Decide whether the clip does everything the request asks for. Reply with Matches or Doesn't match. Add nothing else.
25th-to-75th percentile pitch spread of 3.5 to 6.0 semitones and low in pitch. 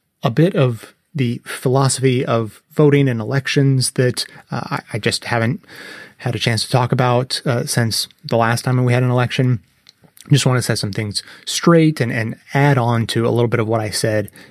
Doesn't match